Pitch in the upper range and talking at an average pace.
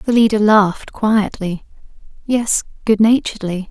No: high, 210 Hz; slow, 95 wpm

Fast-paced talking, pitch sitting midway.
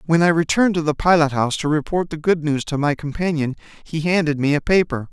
Yes: fast, 235 wpm; medium, 155 Hz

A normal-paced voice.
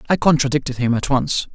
Yes: average, 195 wpm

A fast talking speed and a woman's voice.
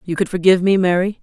Yes: fast, 245 wpm; female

